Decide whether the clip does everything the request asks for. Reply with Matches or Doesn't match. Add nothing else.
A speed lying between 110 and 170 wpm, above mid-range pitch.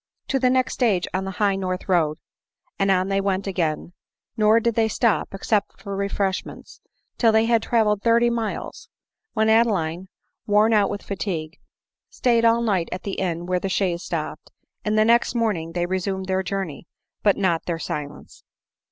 Doesn't match